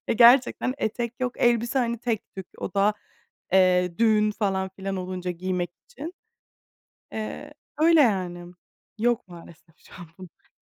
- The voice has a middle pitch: No, high, 210 Hz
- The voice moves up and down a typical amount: Yes, average, 4.6 semitones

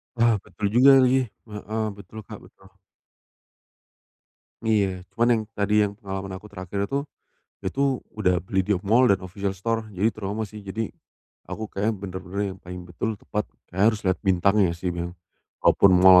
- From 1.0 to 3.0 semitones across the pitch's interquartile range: Yes, average, 2.7 semitones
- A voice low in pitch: Yes, low, 100 Hz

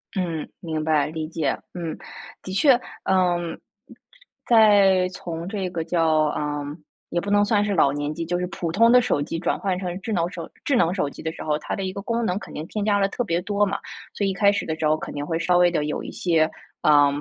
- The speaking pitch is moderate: Yes, medium, 175 Hz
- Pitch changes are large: No, average, 4.0 semitones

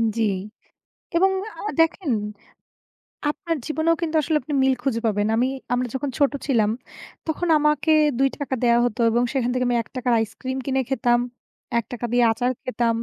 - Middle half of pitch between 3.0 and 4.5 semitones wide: Yes, average, 3.7 semitones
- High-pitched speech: Yes, very high, 260 Hz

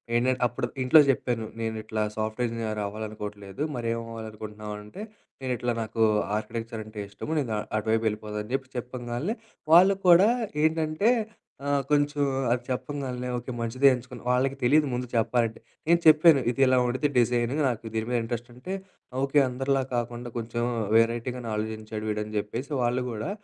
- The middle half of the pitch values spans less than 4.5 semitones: Yes, average, 3.2 semitones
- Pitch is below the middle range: Yes, low, 120 Hz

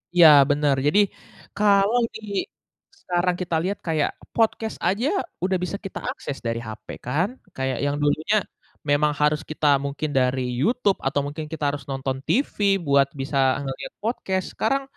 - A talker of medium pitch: Yes, medium, 155 Hz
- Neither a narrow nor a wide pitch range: No, wide, 6.2 semitones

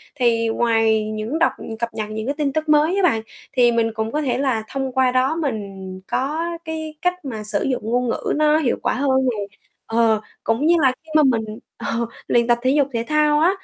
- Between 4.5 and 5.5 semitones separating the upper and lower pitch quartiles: Yes, average, 5.0 semitones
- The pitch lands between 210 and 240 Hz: No, very high, 250 Hz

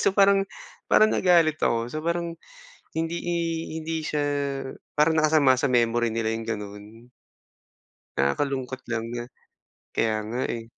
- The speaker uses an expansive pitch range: Yes, wide, 6.0 semitones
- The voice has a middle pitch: No, low, 130 Hz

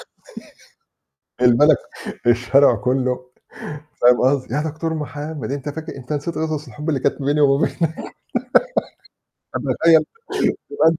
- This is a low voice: No, medium, 145 Hz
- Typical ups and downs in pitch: Yes, average, 3.5 semitones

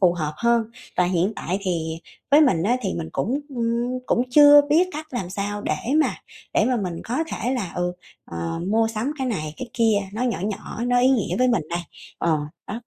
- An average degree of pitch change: No, wide, 5.9 semitones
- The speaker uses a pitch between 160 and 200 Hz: No, high, 225 Hz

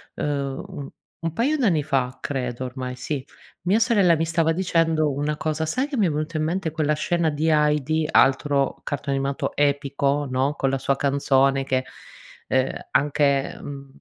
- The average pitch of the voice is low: No, medium, 145 Hz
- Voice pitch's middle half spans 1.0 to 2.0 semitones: No, average, 2.7 semitones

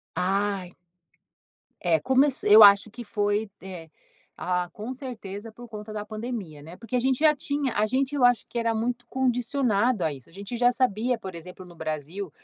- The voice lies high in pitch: Yes, high, 215 Hz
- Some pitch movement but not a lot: Yes, average, 4.5 semitones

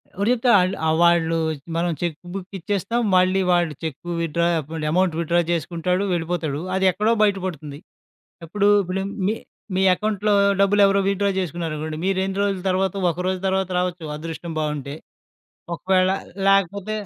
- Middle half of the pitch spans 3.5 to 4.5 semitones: No, average, 2.9 semitones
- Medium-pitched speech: Yes, medium, 180 Hz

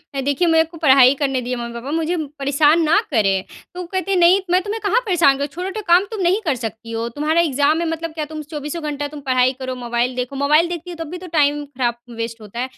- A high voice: Yes, very high, 295 Hz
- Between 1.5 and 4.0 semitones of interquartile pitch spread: No, average, 5.0 semitones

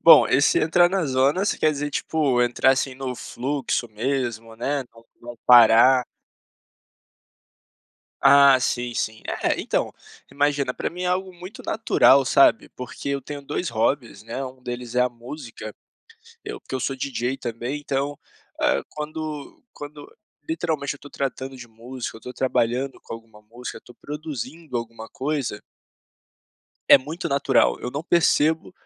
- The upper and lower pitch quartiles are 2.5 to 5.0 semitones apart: Yes, average, 3.4 semitones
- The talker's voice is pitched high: No, low, 135 Hz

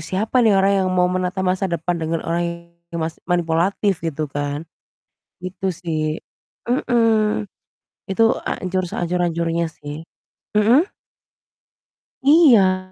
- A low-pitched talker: No, medium, 180 Hz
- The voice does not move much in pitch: No, average, 3.7 semitones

